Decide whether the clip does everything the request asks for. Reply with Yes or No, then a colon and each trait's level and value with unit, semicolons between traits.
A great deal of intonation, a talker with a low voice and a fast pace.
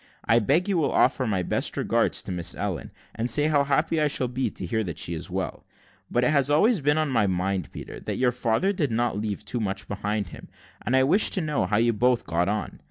Yes: wide, 6.3 semitones; low, 120 Hz; fast, 245 wpm